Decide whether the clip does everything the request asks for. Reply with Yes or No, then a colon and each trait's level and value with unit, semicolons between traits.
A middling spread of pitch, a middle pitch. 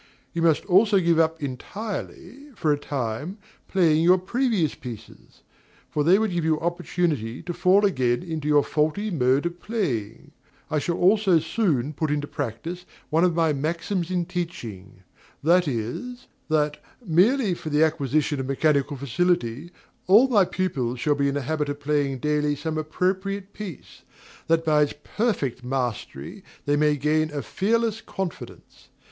Yes: average, 4.2 semitones; medium, 160 Hz